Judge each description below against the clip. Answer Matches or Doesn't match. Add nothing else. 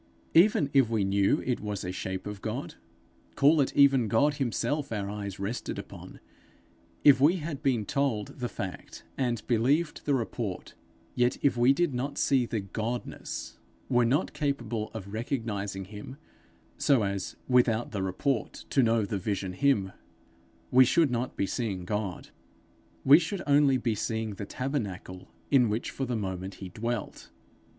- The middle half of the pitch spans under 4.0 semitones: Doesn't match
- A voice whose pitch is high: Doesn't match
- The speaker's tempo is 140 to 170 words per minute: Matches